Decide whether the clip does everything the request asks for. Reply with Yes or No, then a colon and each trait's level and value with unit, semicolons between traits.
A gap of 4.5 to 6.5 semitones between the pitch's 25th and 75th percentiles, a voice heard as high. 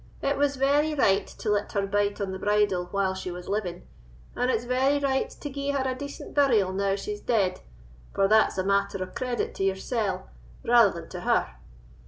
Yes: wide, 5.4 semitones; high, 210 Hz